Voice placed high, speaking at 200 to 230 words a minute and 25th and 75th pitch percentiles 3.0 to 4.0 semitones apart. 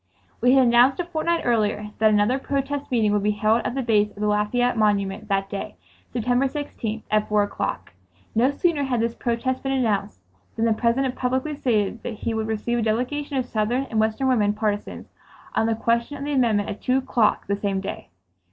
Yes: high, 230 Hz; fast, 205 wpm; average, 3.6 semitones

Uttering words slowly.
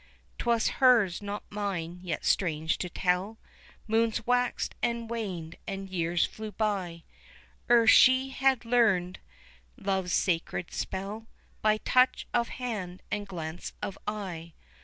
Yes: slow, 125 wpm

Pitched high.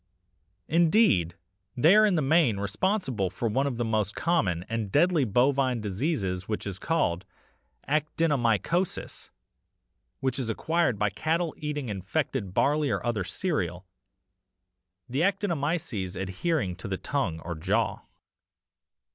No: low, 125 Hz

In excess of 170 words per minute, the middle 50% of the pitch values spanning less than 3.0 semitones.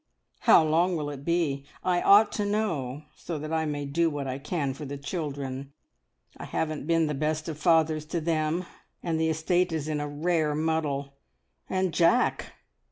Yes: average, 180 wpm; narrow, 2.6 semitones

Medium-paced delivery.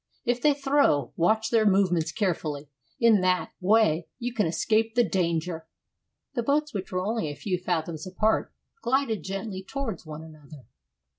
Yes: average, 155 wpm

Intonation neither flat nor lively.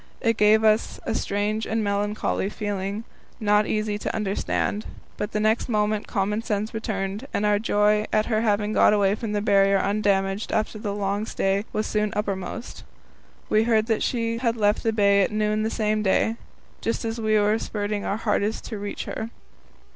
No: narrow, 1.2 semitones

